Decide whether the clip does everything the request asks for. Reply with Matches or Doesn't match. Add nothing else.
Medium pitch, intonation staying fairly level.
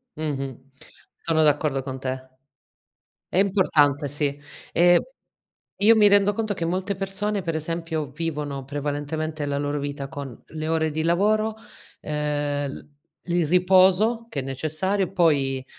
Doesn't match